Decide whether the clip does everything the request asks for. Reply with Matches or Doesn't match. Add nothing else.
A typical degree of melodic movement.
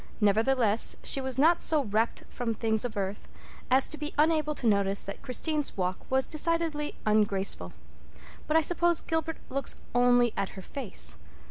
Doesn't match